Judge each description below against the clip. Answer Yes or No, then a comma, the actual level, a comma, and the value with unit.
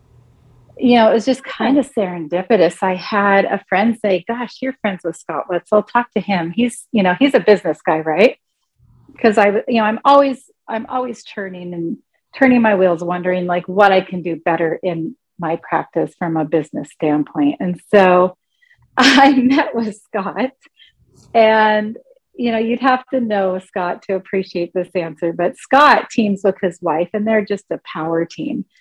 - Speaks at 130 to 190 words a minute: Yes, average, 185 wpm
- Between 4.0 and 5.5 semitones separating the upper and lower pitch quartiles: Yes, average, 5.1 semitones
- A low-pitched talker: No, high, 200 Hz